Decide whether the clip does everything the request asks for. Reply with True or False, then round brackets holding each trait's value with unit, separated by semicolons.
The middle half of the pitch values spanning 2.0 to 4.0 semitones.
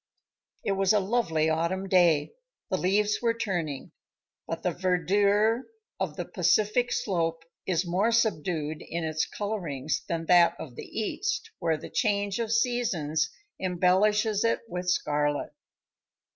False (4.4 semitones)